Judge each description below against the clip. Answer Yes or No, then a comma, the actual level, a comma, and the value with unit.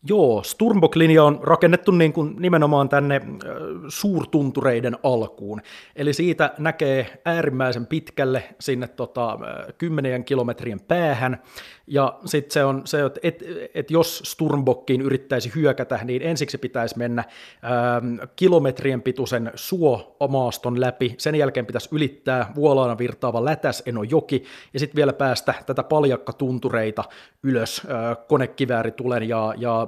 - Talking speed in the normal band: Yes, average, 125 wpm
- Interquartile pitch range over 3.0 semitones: Yes, average, 3.7 semitones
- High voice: No, low, 135 Hz